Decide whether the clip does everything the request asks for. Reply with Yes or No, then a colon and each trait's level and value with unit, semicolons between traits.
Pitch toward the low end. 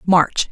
No: medium, 165 Hz